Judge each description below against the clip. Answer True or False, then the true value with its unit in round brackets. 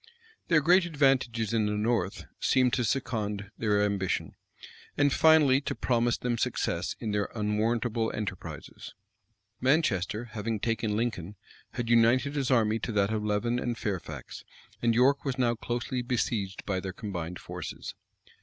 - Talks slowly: False (145 wpm)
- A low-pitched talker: True (115 Hz)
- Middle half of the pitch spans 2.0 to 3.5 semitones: True (3.2 semitones)